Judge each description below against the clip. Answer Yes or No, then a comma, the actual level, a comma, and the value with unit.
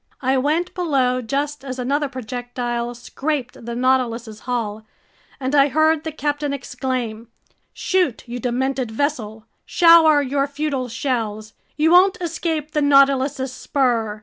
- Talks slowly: Yes, slow, 130 wpm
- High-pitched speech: Yes, very high, 265 Hz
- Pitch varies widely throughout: No, average, 3.4 semitones